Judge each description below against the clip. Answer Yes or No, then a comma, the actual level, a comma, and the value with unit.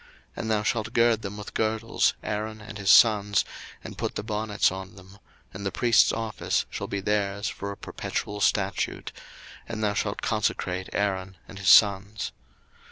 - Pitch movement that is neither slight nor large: No, narrow, 1.8 semitones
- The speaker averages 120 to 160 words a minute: No, average, 170 wpm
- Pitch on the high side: No, low, 105 Hz